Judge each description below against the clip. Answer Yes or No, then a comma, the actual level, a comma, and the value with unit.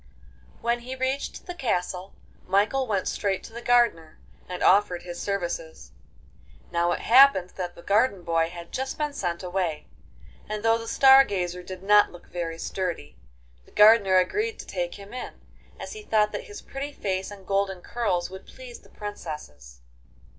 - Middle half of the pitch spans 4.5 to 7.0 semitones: Yes, average, 5.1 semitones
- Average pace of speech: Yes, average, 170 wpm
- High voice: Yes, high, 195 Hz